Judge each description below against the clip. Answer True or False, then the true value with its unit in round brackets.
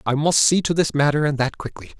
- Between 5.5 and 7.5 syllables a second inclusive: True (6.0 syllables/s)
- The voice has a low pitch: False (150 Hz)